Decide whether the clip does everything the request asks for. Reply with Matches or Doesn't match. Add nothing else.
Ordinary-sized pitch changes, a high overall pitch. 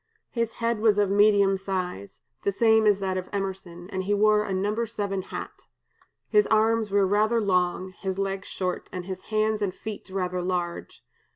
Doesn't match